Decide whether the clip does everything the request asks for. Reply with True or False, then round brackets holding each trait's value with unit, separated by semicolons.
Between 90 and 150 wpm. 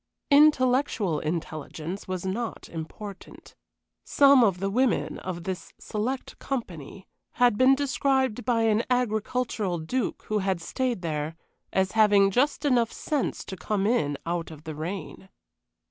True (135 wpm)